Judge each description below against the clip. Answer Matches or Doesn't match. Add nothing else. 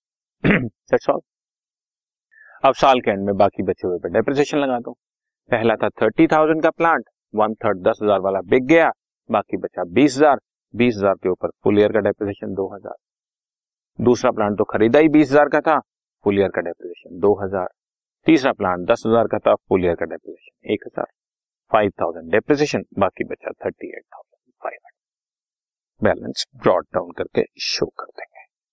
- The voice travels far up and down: Matches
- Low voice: Matches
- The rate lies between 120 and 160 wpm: Matches